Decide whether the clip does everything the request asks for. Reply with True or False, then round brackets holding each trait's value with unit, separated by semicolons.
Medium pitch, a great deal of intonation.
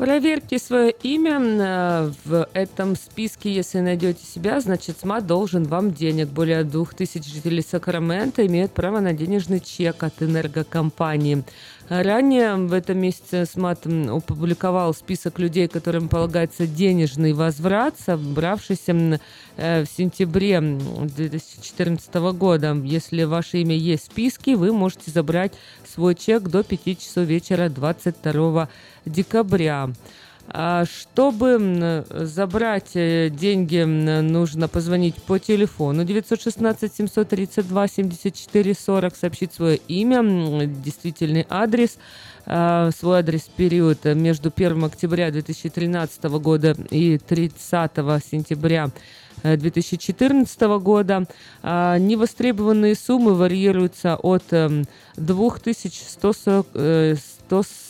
False (175 Hz; 3.4 semitones)